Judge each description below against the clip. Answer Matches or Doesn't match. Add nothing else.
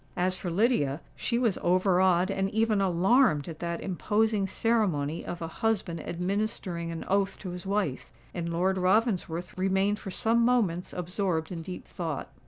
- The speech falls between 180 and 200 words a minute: Doesn't match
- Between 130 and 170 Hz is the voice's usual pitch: Doesn't match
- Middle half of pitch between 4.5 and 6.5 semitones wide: Doesn't match